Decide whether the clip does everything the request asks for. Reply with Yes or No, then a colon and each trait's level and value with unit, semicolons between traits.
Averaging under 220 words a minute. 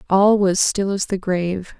Yes: average, 200 wpm